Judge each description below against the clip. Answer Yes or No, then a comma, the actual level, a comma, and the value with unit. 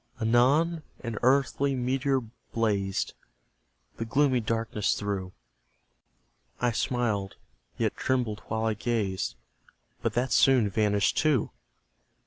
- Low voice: Yes, low, 115 Hz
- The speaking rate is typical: No, slow, 105 wpm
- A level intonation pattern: No, average, 3.6 semitones